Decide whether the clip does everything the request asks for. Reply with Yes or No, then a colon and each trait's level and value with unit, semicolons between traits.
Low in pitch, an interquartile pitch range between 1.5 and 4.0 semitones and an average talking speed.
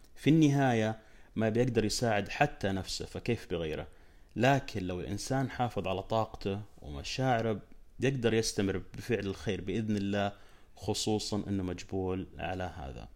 Yes: low, 100 Hz; average, 3.5 semitones; average, 125 wpm